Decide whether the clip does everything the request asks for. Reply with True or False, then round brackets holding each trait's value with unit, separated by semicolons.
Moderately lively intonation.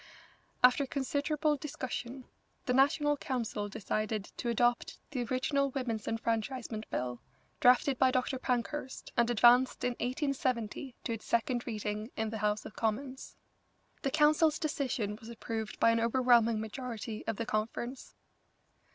True (3.1 semitones)